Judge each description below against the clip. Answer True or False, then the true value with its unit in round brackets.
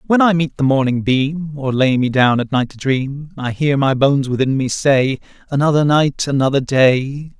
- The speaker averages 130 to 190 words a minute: False (205 wpm)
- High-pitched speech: False (140 Hz)